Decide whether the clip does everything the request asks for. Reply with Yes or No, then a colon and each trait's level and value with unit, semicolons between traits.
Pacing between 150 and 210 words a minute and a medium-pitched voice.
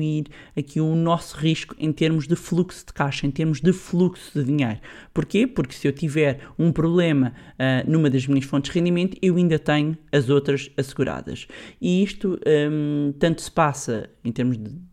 Yes: average, 180 wpm; medium, 155 Hz